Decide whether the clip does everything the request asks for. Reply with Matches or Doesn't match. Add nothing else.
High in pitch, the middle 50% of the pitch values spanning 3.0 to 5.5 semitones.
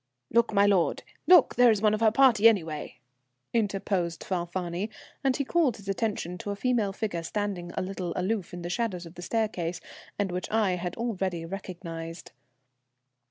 Matches